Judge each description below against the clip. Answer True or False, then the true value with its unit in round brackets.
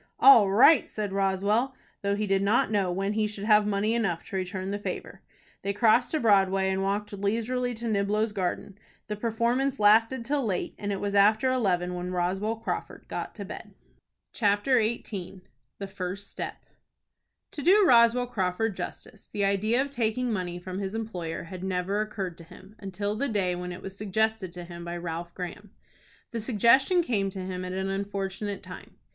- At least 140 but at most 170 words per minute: False (185 wpm)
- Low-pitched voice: False (205 Hz)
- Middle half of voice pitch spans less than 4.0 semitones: True (2.9 semitones)